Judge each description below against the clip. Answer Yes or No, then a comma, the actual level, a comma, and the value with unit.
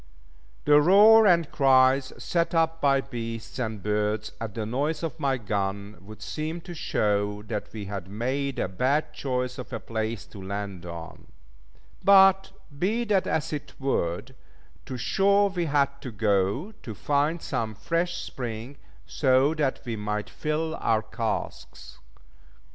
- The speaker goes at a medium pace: Yes, average, 150 wpm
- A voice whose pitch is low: Yes, low, 130 Hz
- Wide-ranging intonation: Yes, wide, 6.6 semitones